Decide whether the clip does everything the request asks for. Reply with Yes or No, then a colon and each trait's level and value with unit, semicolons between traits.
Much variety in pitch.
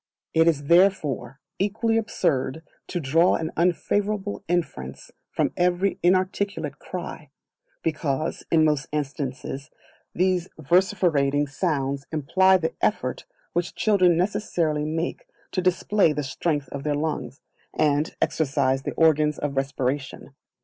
No: average, 4.3 semitones